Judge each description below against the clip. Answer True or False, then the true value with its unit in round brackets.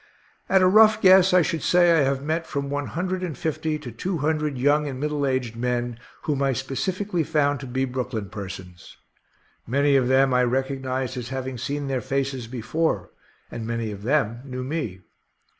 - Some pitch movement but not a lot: True (3.8 semitones)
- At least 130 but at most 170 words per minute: False (190 wpm)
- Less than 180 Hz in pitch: True (135 Hz)